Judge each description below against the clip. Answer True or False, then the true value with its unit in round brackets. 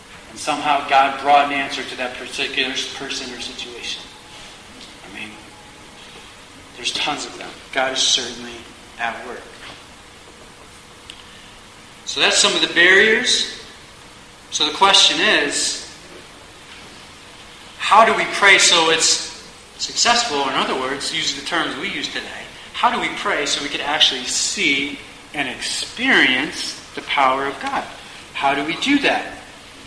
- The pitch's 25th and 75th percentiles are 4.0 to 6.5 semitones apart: True (4.3 semitones)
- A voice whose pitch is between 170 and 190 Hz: False (135 Hz)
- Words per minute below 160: True (135 wpm)